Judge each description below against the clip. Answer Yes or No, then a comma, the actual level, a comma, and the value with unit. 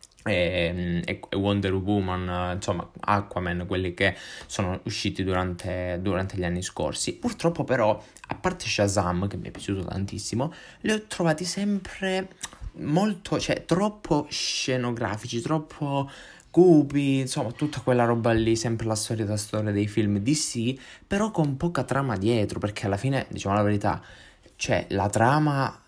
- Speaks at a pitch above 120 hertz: No, low, 110 Hz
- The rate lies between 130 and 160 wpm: Yes, average, 145 wpm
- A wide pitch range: Yes, wide, 6.6 semitones